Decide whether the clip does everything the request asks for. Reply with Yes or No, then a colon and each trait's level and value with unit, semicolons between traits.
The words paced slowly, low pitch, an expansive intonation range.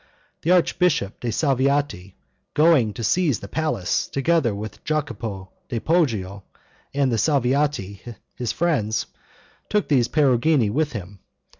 Yes: slow, 125 wpm; low, 130 Hz; wide, 6.1 semitones